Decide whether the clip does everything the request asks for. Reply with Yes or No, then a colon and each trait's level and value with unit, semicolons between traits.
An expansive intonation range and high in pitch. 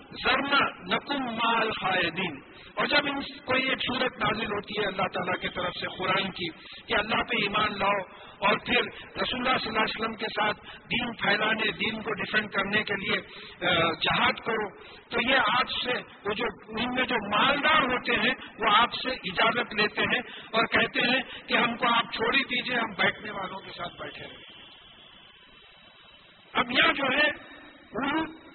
No: average, 3.9 semitones; high, 220 Hz